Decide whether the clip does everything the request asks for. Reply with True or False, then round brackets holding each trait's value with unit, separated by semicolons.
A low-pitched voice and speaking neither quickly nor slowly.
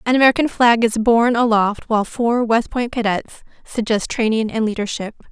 False (230 Hz; 170 wpm)